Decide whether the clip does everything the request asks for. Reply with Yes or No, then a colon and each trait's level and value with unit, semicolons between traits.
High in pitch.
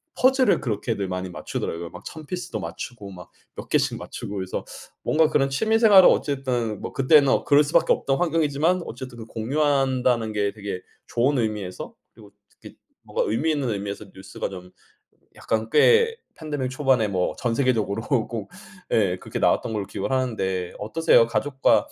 No: low, 120 Hz